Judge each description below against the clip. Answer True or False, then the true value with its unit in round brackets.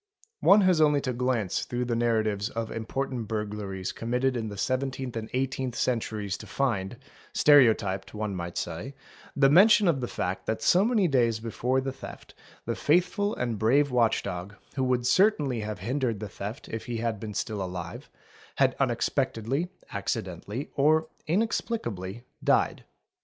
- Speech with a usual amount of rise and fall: True (4.4 semitones)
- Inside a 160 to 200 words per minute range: True (165 wpm)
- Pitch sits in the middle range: False (120 Hz)